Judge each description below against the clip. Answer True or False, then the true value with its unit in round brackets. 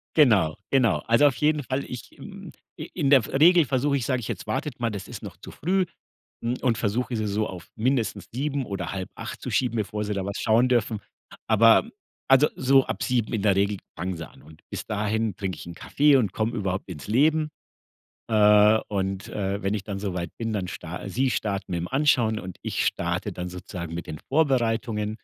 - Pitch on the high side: False (110 Hz)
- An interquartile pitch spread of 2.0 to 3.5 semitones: False (5.0 semitones)